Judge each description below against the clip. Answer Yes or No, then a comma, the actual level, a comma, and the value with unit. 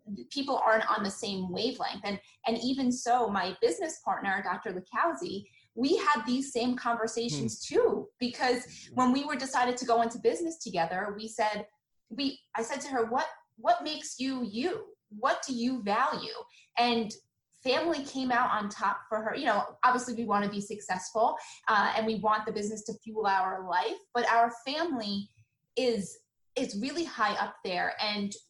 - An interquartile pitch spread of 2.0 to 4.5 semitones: Yes, average, 4.1 semitones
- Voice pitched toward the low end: No, high, 235 Hz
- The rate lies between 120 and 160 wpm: No, average, 175 wpm